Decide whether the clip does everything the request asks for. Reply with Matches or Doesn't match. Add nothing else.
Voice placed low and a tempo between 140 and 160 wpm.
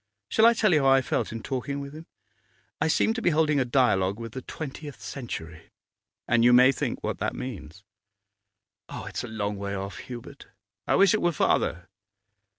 Doesn't match